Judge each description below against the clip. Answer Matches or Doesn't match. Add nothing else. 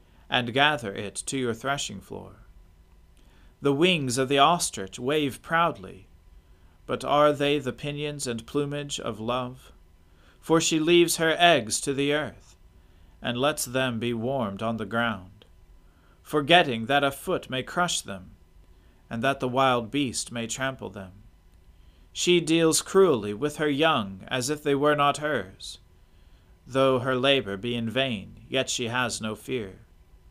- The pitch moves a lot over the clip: Matches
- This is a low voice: Matches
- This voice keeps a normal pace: Matches